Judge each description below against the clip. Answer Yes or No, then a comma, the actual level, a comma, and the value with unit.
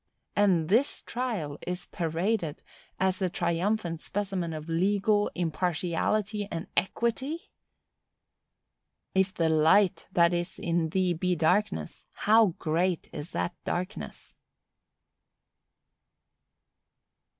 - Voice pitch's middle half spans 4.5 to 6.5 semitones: No, average, 3.6 semitones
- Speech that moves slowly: Yes, slow, 95 wpm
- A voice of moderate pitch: Yes, medium, 180 Hz